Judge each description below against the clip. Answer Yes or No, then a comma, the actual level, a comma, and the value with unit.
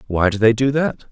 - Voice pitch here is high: No, low, 120 Hz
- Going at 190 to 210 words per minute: No, fast, 270 wpm